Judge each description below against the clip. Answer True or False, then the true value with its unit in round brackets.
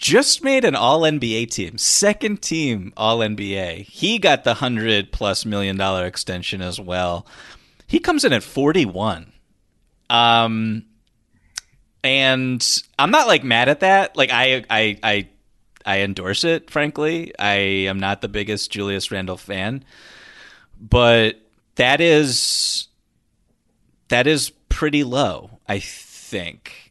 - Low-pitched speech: True (115 Hz)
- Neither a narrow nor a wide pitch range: False (6.4 semitones)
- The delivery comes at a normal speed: False (125 wpm)